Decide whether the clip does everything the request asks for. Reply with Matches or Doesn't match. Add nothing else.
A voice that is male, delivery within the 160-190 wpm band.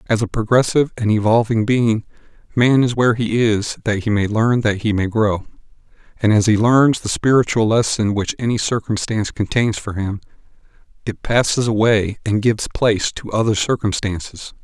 Matches